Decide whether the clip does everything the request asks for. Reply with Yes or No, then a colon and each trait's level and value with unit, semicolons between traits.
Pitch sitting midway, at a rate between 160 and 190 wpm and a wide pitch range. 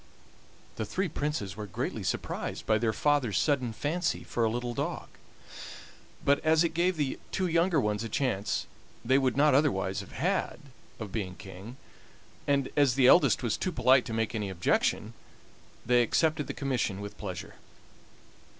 No: low, 125 Hz; average, 165 wpm; wide, 5.7 semitones